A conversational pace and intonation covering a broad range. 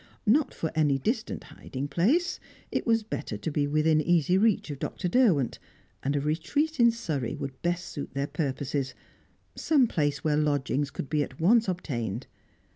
Yes: average, 170 wpm; wide, 7.2 semitones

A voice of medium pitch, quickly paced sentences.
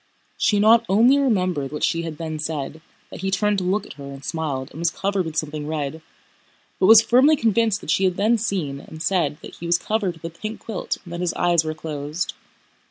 Yes: medium, 175 Hz; fast, 220 wpm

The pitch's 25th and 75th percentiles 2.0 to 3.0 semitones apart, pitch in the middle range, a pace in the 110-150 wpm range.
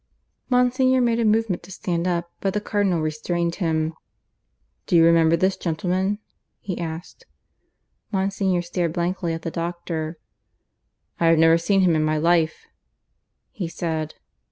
Yes: average, 2.7 semitones; medium, 175 Hz; average, 145 wpm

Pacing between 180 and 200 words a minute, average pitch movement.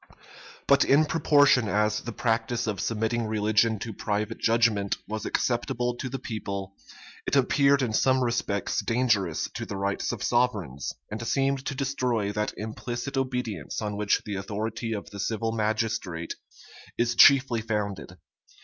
No: average, 150 wpm; average, 3.1 semitones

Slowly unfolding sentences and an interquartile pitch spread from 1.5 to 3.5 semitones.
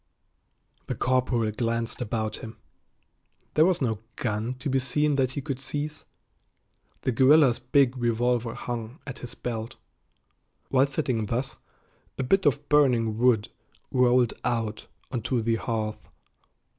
Yes: slow, 130 wpm; average, 2.8 semitones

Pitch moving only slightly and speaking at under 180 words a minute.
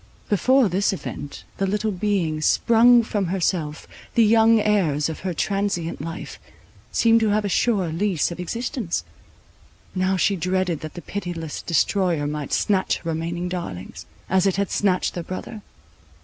No: average, 3.7 semitones; average, 155 wpm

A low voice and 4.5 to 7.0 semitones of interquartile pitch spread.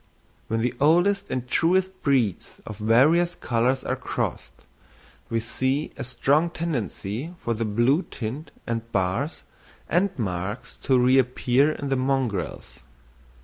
Yes: low, 130 Hz; average, 5.1 semitones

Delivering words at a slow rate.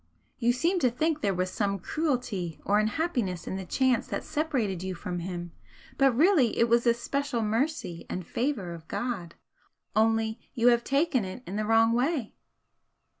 No: average, 175 wpm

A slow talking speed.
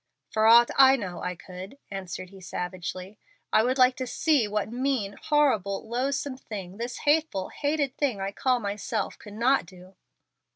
No: average, 165 wpm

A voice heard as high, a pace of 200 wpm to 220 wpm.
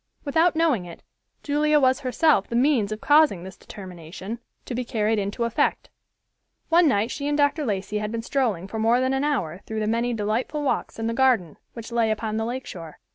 Yes: high, 230 Hz; fast, 205 wpm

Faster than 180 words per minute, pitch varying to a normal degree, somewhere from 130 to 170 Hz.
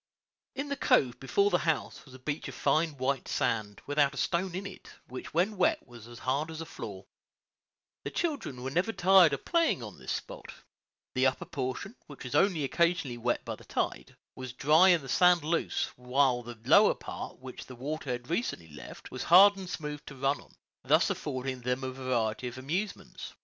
No: average, 200 wpm; wide, 5.7 semitones; medium, 140 Hz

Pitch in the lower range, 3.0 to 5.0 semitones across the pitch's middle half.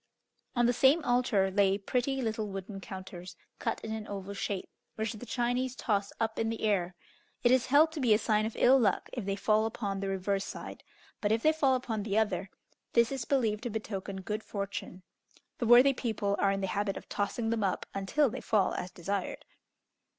No: high, 215 Hz; average, 3.5 semitones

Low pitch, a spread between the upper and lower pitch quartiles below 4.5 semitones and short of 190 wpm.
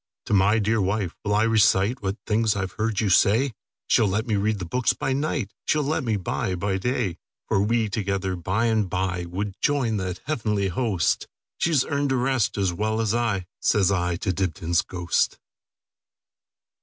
Yes: low, 105 Hz; average, 3.3 semitones; average, 170 wpm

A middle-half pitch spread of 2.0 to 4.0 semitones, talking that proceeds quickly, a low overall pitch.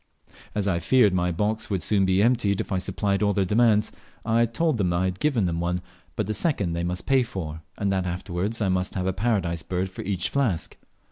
Yes: average, 3.3 semitones; fast, 230 wpm; very low, 95 Hz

